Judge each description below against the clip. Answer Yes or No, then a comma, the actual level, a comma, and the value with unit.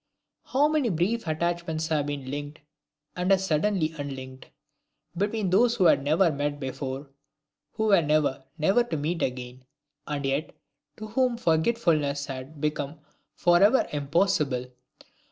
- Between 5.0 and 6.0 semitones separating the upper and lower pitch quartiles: Yes, average, 5.3 semitones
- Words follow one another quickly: No, slow, 135 wpm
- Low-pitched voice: No, medium, 155 Hz